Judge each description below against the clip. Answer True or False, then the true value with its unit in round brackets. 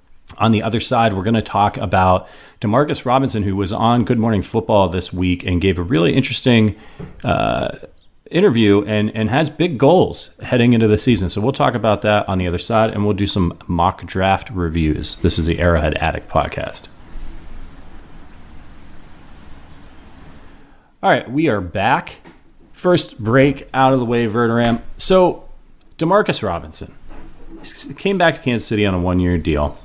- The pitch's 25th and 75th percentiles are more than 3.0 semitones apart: True (5.5 semitones)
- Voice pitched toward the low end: True (100 Hz)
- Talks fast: False (165 wpm)